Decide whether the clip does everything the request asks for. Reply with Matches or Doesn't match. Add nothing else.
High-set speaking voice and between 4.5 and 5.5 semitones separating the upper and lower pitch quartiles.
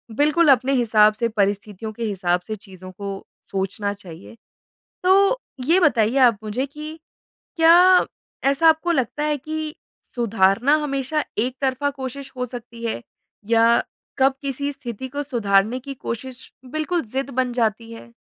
Matches